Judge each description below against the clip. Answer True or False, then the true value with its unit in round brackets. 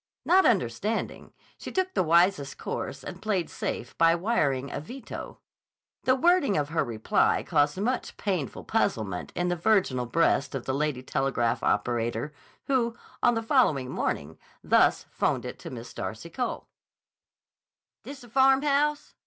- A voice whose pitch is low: False (165 Hz)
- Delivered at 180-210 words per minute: False (145 wpm)